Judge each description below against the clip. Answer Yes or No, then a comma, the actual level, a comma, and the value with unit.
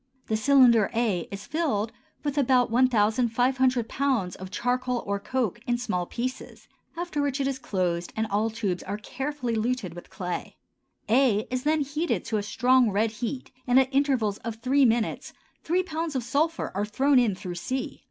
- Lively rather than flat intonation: No, average, 4.0 semitones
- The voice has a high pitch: Yes, high, 245 Hz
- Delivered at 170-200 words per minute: Yes, average, 175 wpm